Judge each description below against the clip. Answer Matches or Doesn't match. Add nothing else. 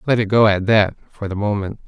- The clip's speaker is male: Matches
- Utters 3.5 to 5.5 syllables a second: Doesn't match